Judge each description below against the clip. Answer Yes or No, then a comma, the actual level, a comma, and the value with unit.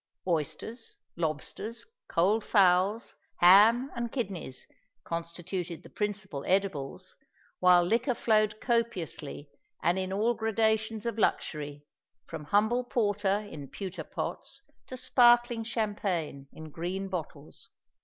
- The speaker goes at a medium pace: No, slow, 110 wpm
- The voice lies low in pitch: No, high, 195 Hz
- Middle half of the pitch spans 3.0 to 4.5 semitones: No, average, 4.9 semitones